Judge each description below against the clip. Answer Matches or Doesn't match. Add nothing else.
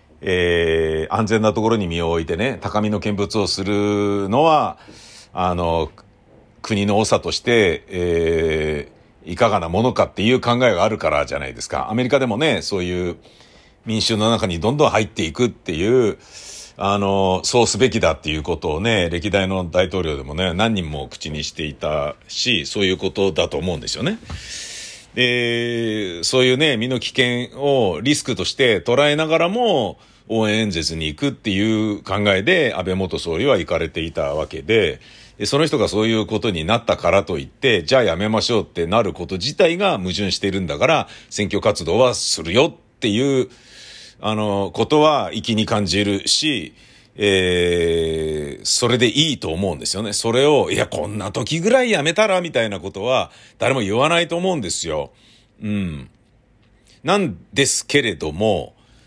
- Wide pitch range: Doesn't match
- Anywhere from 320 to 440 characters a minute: Matches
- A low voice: Matches